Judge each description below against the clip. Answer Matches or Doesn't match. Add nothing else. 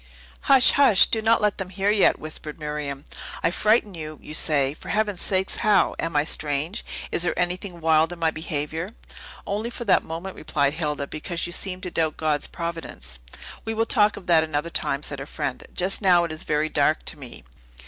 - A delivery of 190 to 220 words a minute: Matches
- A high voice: Doesn't match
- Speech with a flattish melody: Doesn't match